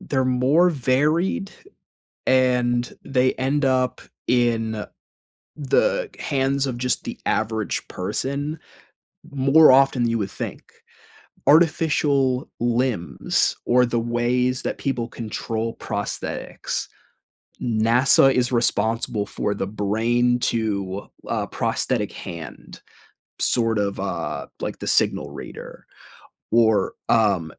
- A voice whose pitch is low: Yes, low, 125 Hz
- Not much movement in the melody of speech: No, average, 3.3 semitones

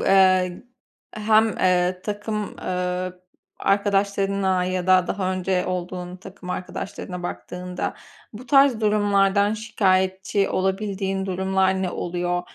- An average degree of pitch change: No, narrow, 1.8 semitones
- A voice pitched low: No, high, 190 Hz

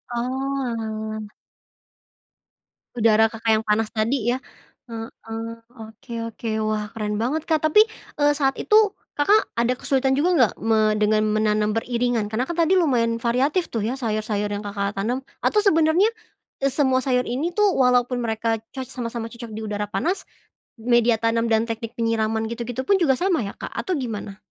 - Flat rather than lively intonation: No, average, 3.5 semitones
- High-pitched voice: Yes, high, 235 Hz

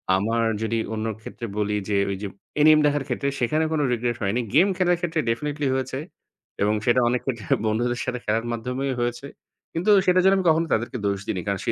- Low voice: Yes, low, 120 Hz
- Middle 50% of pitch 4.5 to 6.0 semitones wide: Yes, average, 5.0 semitones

